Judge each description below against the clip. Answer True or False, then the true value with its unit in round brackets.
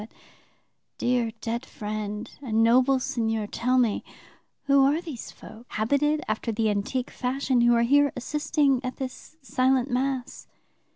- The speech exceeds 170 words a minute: False (140 wpm)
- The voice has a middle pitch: False (250 Hz)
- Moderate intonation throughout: True (3.1 semitones)